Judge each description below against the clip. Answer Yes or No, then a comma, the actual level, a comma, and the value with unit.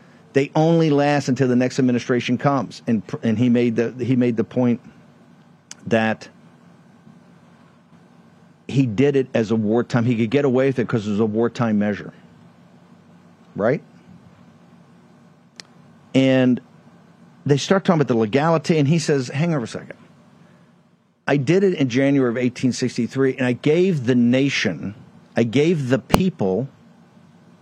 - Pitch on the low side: Yes, low, 130 Hz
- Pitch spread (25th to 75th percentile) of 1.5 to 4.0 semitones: Yes, average, 3.1 semitones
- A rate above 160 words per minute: No, average, 145 wpm